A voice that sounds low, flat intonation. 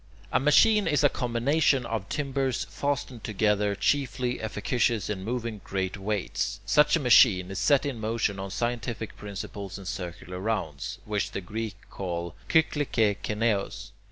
No: low, 110 Hz; average, 4.2 semitones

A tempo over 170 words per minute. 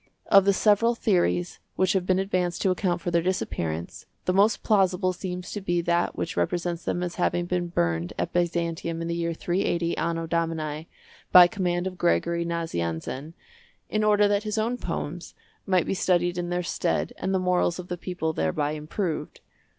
Yes: average, 180 wpm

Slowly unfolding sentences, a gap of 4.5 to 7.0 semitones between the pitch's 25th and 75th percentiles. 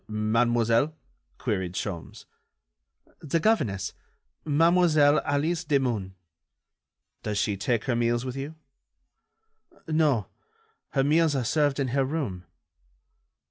Yes: slow, 100 wpm; wide, 5.6 semitones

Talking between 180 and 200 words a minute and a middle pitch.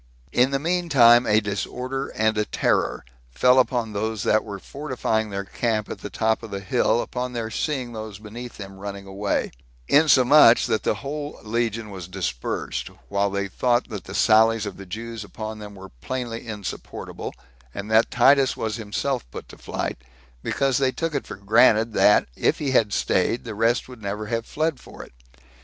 No: average, 185 wpm; low, 110 Hz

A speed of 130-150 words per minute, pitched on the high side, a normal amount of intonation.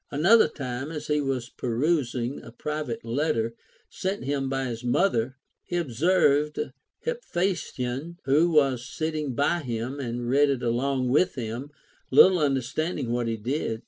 No: average, 145 wpm; low, 135 Hz; average, 4.1 semitones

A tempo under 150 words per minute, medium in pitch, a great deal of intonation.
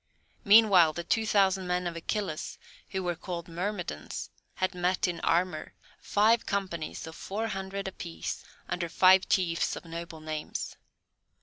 No: average, 140 wpm; medium, 180 Hz; average, 2.7 semitones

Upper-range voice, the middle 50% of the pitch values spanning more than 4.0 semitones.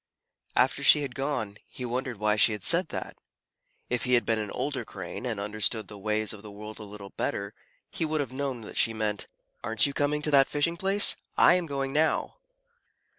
No: low, 120 Hz; average, 5.1 semitones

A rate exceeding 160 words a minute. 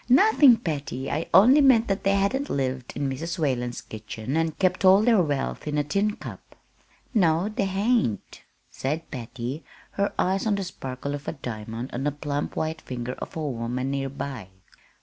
Yes: average, 180 wpm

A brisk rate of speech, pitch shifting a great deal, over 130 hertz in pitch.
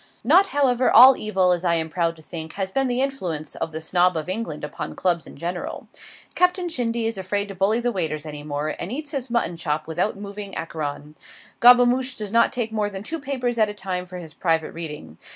Yes: fast, 220 wpm; wide, 6.7 semitones; high, 190 Hz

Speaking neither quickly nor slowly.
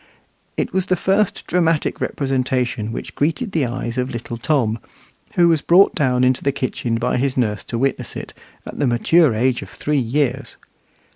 Yes: average, 180 wpm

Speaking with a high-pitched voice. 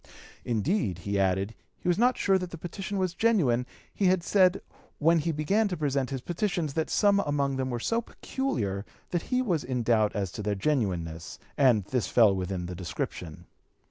No: medium, 140 Hz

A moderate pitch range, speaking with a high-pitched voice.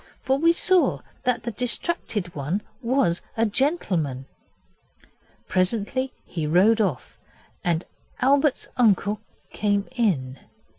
No: wide, 6.7 semitones; high, 210 Hz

